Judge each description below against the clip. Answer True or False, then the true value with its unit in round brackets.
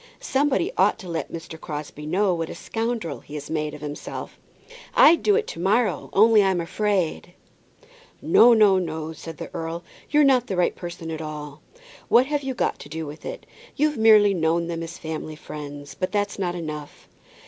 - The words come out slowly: False (190 wpm)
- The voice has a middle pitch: True (175 Hz)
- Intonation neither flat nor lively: False (5.8 semitones)